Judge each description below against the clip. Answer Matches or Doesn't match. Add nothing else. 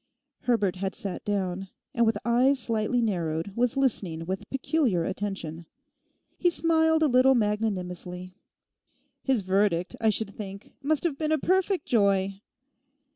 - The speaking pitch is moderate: Doesn't match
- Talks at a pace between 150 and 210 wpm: Doesn't match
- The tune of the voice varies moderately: Doesn't match